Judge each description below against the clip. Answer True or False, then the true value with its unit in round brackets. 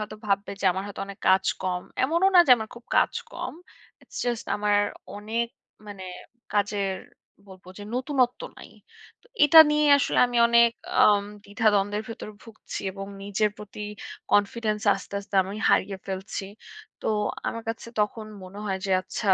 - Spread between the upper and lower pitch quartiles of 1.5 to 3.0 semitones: True (2.7 semitones)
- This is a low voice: False (210 Hz)